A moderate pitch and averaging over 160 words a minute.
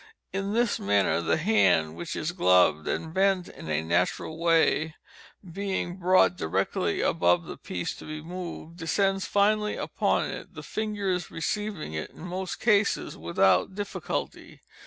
No: medium, 175 Hz; average, 145 wpm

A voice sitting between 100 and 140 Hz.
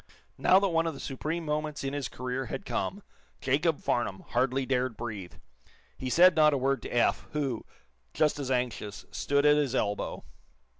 Yes: low, 135 Hz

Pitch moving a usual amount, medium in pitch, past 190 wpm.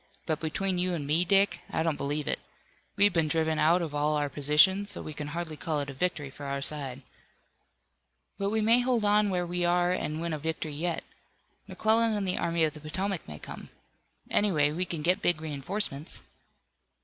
Yes: average, 3.8 semitones; medium, 165 Hz; average, 200 wpm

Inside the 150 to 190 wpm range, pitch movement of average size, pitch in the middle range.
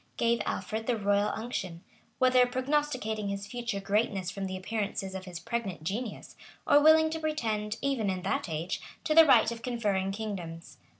No: average, 170 wpm; average, 4.2 semitones; high, 215 Hz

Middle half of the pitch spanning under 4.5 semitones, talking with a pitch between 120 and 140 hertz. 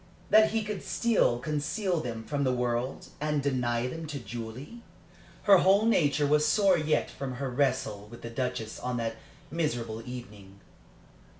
No: average, 4.9 semitones; low, 135 Hz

